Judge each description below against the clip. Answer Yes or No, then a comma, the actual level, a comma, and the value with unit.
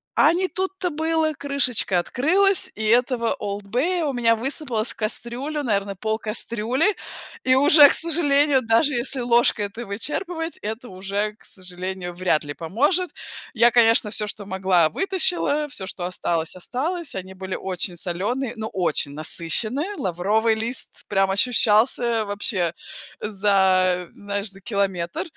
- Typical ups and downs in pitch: No, wide, 6.5 semitones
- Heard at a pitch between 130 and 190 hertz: No, high, 220 Hz